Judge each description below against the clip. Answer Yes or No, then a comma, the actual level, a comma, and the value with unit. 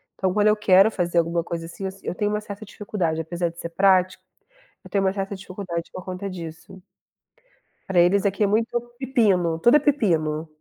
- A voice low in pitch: No, high, 190 Hz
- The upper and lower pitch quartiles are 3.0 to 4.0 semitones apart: Yes, average, 3.3 semitones